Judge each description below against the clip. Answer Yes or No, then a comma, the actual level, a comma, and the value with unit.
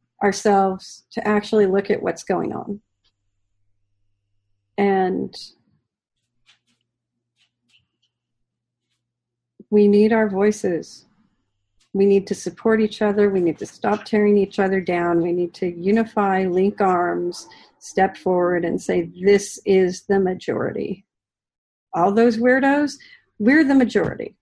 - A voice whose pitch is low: No, medium, 185 Hz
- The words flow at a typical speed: No, slow, 115 wpm